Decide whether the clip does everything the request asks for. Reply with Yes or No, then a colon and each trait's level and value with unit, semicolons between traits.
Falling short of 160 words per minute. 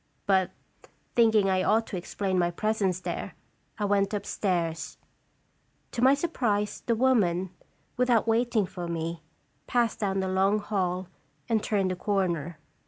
Yes: average, 140 wpm